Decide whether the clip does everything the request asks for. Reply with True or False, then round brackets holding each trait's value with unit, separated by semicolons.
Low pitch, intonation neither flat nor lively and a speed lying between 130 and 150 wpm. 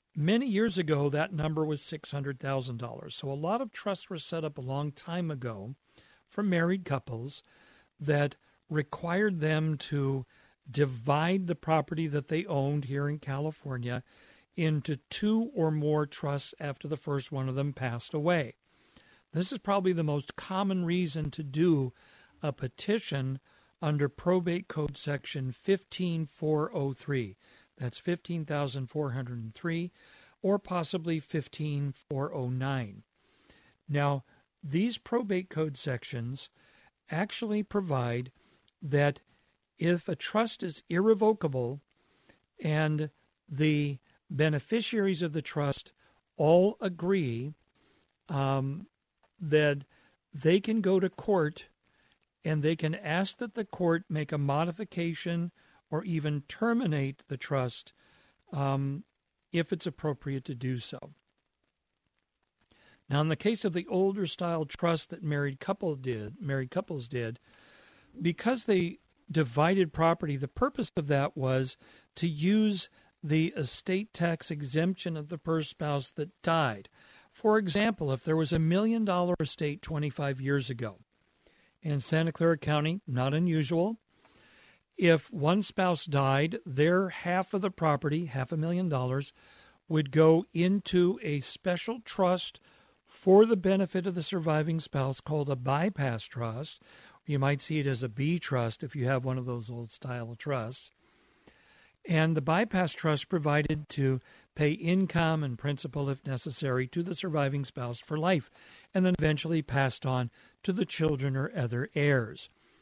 False (155 Hz; 4.2 semitones; 135 wpm)